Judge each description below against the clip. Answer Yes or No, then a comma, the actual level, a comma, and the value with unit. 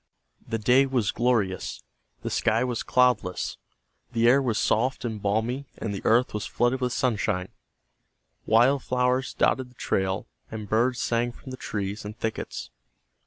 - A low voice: Yes, low, 120 Hz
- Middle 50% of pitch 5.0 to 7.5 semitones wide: No, average, 3.0 semitones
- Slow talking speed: No, average, 155 wpm